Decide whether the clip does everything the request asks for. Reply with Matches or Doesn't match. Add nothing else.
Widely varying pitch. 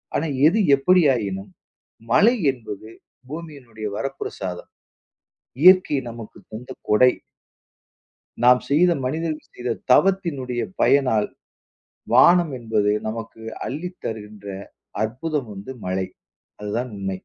Matches